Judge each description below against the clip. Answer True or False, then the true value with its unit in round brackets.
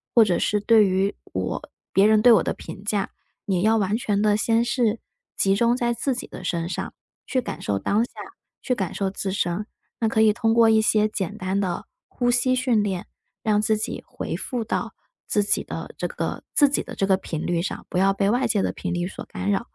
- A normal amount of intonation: True (3.0 semitones)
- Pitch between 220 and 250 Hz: False (210 Hz)